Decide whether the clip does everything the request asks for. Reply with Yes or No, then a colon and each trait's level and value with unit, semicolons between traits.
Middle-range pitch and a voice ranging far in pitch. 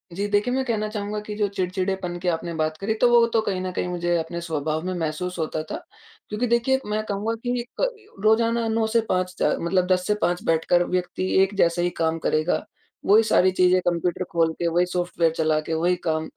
No: medium, 180 Hz; average, 3.8 semitones